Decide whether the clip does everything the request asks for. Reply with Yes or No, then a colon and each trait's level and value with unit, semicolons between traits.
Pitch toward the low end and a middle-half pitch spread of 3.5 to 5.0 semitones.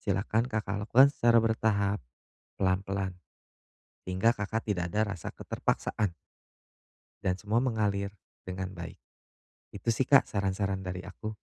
No: low, 100 Hz; narrow, 2.6 semitones